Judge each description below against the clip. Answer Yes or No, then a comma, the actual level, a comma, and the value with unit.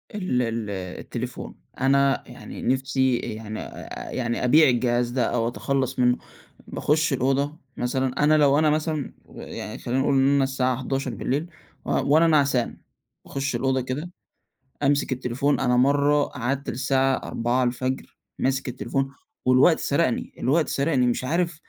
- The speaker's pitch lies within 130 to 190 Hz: Yes, low, 135 Hz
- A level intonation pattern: Yes, narrow, 2.3 semitones